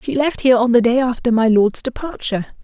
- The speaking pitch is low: No, high, 245 Hz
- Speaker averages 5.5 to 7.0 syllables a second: Yes, 6.3 syllables/s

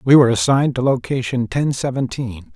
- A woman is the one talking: No, male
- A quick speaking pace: No, average, 165 wpm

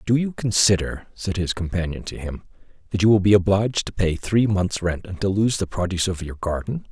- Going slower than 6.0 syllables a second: Yes, 5.6 syllables/s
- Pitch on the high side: No, very low, 95 Hz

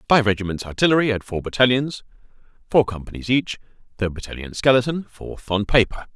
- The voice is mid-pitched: No, low, 115 Hz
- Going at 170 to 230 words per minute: No, average, 145 wpm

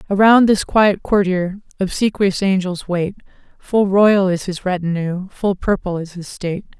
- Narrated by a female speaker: Yes, female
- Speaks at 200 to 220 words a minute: No, average, 150 wpm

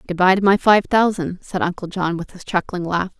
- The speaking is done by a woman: Yes, female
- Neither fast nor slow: No, fast, 245 wpm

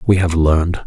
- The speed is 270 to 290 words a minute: No, fast, 210 wpm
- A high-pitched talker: No, very low, 85 Hz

